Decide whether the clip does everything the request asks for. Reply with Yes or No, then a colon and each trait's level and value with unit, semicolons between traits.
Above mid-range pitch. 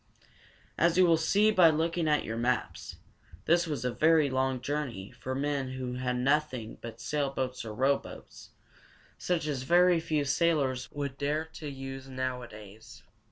No: medium, 140 Hz